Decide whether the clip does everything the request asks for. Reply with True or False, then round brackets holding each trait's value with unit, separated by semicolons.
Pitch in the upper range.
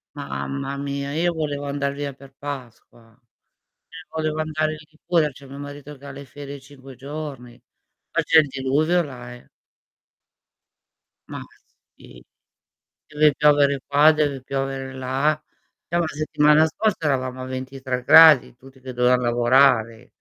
False (140 Hz)